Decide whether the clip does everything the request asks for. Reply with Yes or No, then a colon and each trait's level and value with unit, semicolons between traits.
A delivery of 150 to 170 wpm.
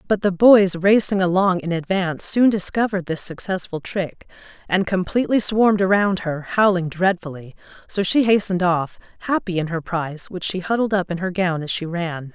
No: average, 180 wpm